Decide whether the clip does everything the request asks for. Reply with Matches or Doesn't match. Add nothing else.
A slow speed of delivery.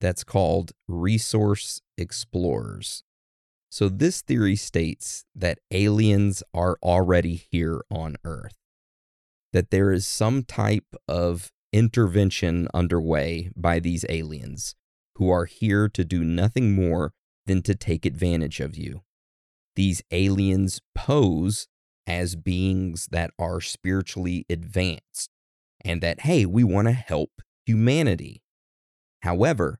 Matches